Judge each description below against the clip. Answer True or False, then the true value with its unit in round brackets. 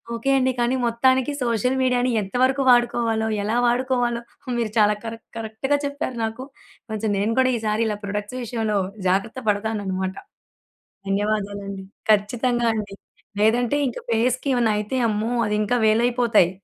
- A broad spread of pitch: False (2.8 semitones)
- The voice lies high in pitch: True (225 Hz)